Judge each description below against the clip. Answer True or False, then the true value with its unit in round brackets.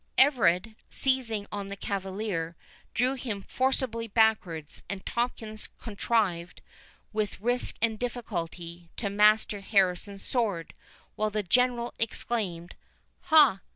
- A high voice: True (215 Hz)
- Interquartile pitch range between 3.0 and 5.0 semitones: True (3.8 semitones)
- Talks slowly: True (110 wpm)